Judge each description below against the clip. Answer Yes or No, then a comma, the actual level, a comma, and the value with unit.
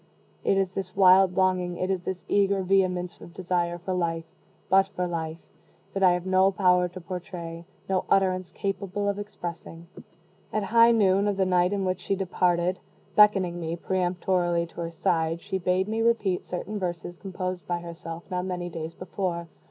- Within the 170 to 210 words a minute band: Yes, average, 175 wpm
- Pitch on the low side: No, medium, 185 Hz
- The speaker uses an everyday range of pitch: No, narrow, 1.8 semitones